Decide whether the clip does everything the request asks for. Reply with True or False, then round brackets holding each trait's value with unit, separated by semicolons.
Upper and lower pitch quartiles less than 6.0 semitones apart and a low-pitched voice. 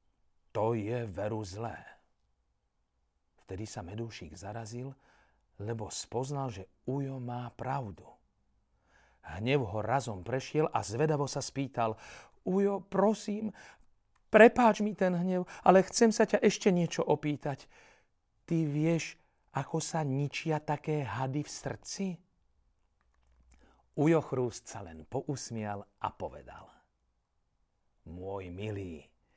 False (7.7 semitones; 125 Hz)